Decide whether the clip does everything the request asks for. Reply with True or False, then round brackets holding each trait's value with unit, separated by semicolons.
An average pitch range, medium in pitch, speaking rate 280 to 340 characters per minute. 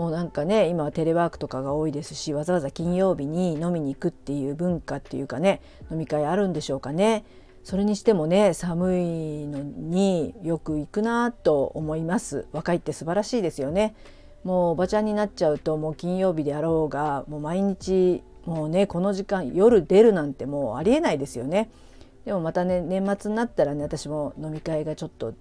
False (4.4 semitones; 170 Hz; 395 characters per minute)